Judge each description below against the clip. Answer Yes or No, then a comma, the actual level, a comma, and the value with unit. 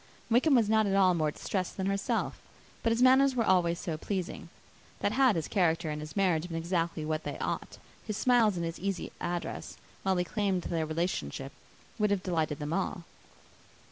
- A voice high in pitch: No, medium, 180 Hz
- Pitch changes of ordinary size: Yes, average, 4.0 semitones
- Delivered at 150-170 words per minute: No, average, 190 wpm